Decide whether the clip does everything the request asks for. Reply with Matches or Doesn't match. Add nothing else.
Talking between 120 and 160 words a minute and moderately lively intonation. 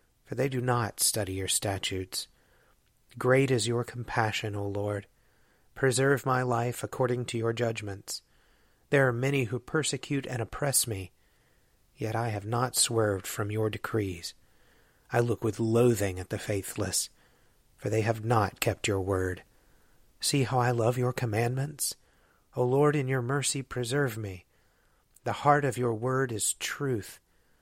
Matches